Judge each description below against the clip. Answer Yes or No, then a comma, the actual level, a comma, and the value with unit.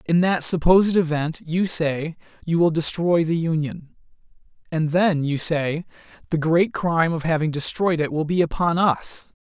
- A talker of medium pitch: Yes, medium, 165 Hz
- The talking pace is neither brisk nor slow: Yes, average, 165 wpm